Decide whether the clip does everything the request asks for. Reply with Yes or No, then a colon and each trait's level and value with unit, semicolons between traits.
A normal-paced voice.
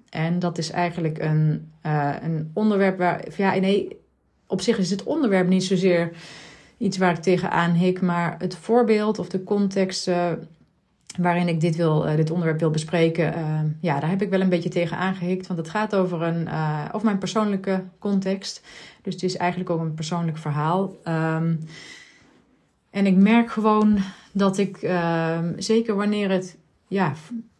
Yes: average, 175 wpm